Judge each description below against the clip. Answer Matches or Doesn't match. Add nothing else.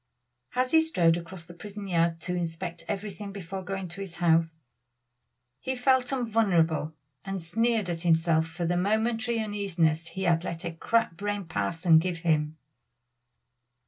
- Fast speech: Doesn't match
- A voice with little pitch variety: Doesn't match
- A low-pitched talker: Doesn't match